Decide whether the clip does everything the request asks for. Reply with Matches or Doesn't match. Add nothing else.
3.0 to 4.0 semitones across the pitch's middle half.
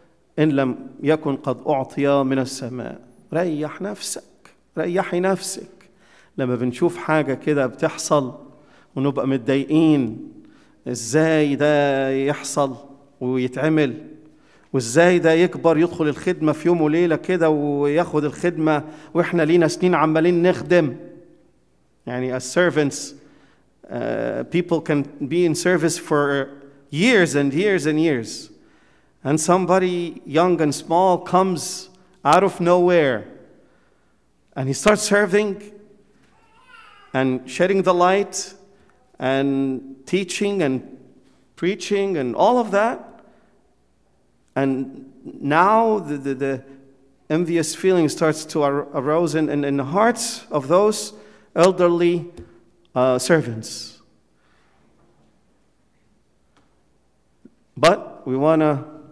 Doesn't match